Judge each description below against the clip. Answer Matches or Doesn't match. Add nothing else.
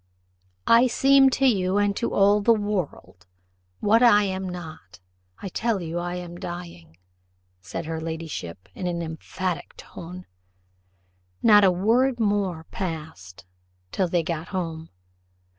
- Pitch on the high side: Doesn't match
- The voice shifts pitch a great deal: Doesn't match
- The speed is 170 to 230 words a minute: Doesn't match